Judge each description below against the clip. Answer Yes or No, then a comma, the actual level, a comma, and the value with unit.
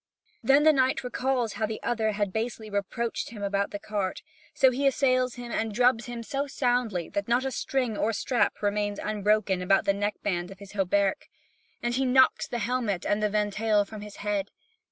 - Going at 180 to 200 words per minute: Yes, average, 195 wpm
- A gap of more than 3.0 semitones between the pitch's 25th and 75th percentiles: Yes, average, 3.5 semitones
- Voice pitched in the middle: No, high, 215 Hz